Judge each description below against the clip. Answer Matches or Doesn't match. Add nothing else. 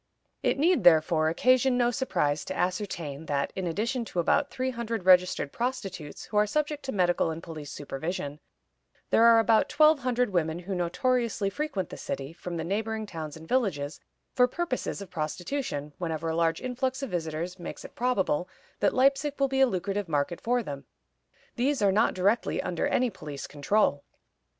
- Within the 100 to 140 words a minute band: Doesn't match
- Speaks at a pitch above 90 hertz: Matches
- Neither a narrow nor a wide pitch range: Doesn't match